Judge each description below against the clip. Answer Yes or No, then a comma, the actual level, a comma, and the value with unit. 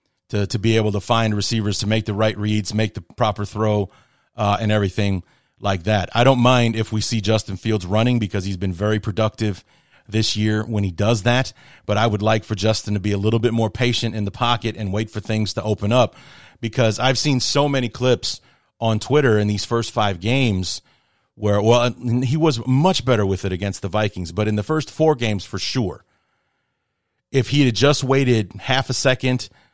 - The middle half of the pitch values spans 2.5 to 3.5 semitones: Yes, average, 3.0 semitones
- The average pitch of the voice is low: Yes, low, 110 Hz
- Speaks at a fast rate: Yes, fast, 210 wpm